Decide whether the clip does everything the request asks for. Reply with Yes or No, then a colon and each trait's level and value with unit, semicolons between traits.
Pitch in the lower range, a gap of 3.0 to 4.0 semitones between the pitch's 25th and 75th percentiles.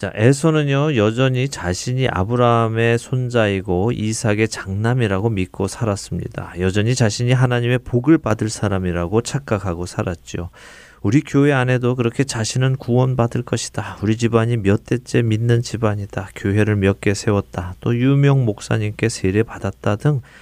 Yes: low, 115 Hz; average, 3.6 semitones